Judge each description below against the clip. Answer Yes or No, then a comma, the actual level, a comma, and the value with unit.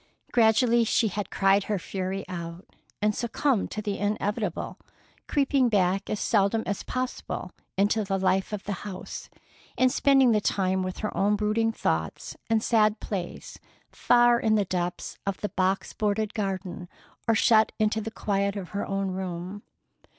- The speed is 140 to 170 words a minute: Yes, average, 160 wpm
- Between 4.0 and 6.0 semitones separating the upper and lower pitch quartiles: No, narrow, 2.6 semitones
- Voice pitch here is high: Yes, high, 205 Hz